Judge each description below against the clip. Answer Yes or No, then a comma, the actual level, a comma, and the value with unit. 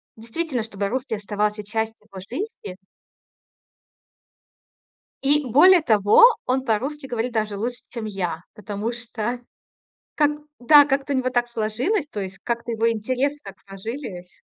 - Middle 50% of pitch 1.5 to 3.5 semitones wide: No, average, 4.0 semitones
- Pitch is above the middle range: Yes, high, 230 Hz